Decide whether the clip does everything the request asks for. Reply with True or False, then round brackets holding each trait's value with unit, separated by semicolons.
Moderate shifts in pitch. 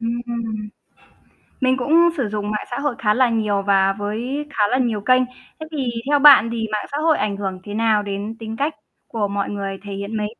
True (3.7 semitones)